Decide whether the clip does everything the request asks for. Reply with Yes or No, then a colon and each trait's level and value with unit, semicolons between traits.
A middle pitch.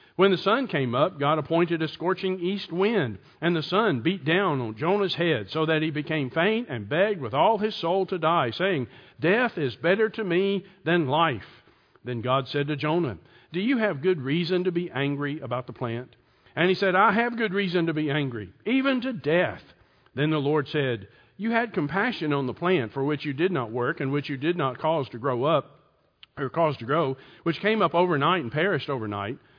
Yes: medium, 160 Hz